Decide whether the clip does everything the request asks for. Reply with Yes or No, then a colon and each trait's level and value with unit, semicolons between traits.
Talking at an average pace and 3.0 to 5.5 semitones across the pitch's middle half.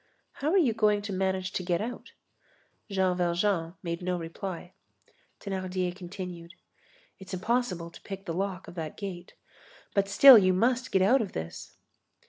No: average, 160 wpm; narrow, 2.6 semitones